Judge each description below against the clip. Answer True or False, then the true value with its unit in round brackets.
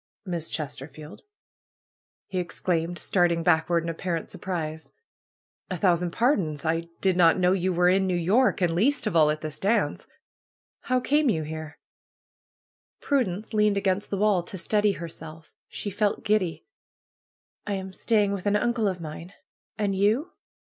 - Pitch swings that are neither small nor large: True (3.8 semitones)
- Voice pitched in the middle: True (180 Hz)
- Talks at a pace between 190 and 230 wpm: False (155 wpm)